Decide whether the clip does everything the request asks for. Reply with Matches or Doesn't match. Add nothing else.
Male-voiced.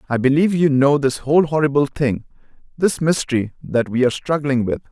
Matches